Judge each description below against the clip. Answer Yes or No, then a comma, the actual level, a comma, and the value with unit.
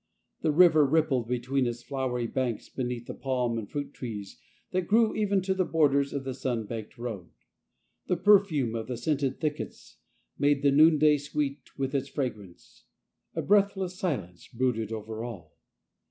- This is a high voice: No, low, 135 Hz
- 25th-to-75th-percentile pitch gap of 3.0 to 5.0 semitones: Yes, average, 4.6 semitones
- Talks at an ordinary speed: Yes, average, 170 wpm